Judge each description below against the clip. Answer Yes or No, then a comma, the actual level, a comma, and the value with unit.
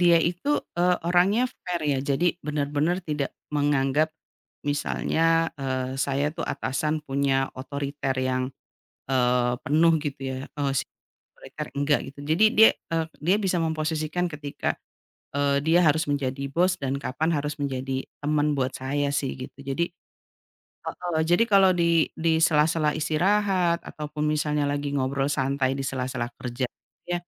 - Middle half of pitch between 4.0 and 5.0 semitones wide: No, average, 3.2 semitones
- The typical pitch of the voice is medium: Yes, medium, 150 Hz